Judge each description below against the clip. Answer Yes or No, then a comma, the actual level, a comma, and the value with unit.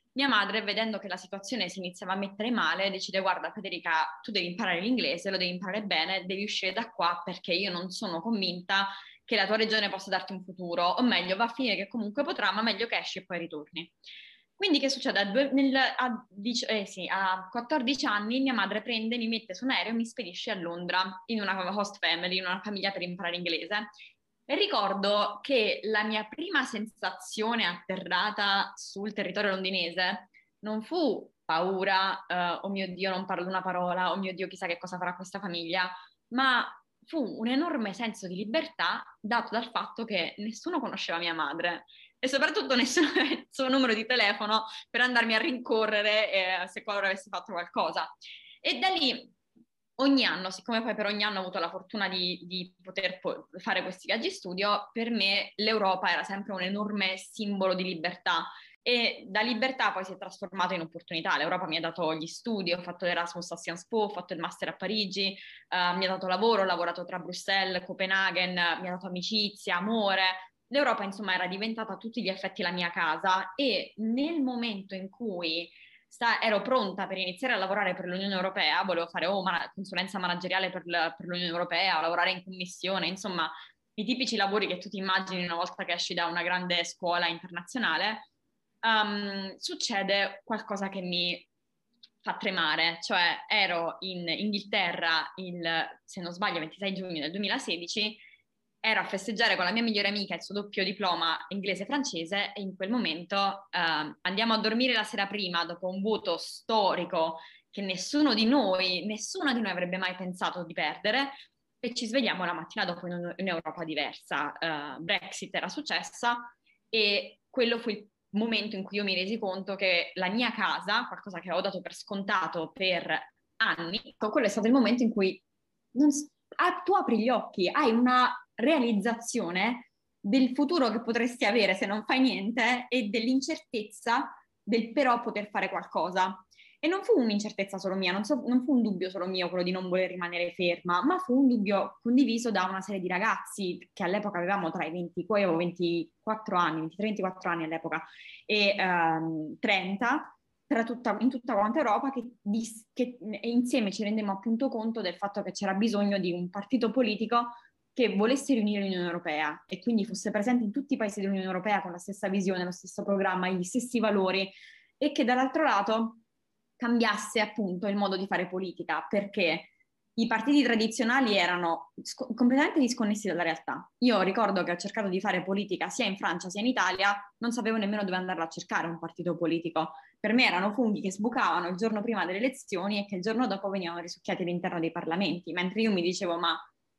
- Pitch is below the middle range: No, high, 200 Hz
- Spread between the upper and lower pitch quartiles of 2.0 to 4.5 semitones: Yes, average, 4.0 semitones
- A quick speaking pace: Yes, fast, 185 wpm